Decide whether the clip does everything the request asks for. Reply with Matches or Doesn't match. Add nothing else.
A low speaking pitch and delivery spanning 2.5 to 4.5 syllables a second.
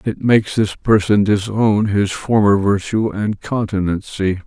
Matches